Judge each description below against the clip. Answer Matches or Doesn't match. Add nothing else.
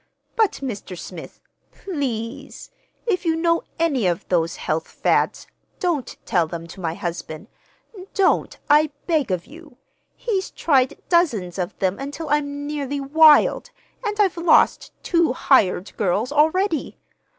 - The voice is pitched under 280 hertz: Doesn't match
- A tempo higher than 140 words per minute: Doesn't match